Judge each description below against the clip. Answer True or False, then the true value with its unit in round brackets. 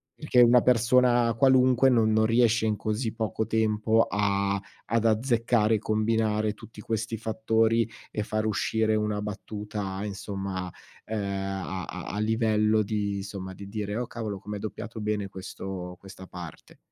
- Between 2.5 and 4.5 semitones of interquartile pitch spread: False (2.1 semitones)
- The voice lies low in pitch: True (110 Hz)